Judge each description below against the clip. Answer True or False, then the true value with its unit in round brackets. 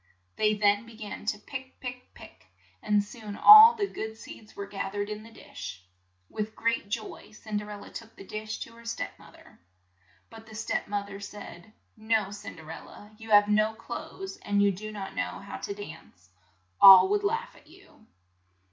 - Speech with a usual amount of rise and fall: False (1.9 semitones)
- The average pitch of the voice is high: True (215 Hz)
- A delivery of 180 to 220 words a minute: True (200 wpm)